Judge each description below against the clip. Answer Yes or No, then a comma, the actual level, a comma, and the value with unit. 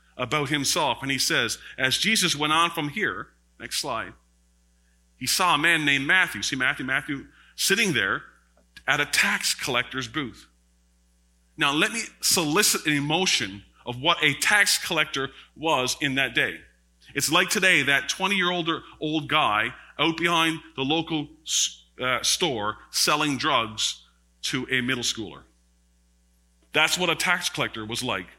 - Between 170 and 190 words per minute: No, average, 150 wpm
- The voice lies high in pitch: No, low, 135 Hz